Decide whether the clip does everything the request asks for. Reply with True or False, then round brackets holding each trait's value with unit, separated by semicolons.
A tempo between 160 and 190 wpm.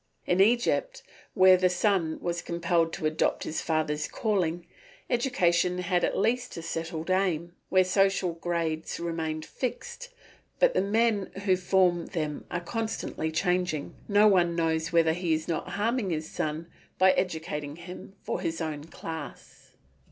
False (150 wpm)